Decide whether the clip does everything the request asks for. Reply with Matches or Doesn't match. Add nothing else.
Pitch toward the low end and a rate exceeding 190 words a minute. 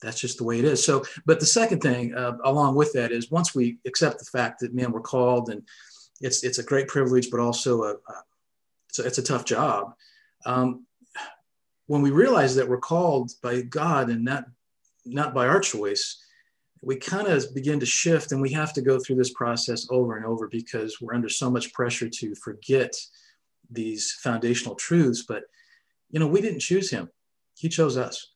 Matches